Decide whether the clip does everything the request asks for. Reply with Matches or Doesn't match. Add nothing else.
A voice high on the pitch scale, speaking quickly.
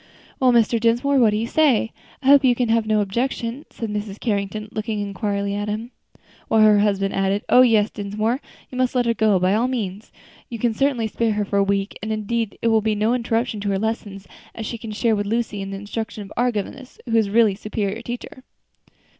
Matches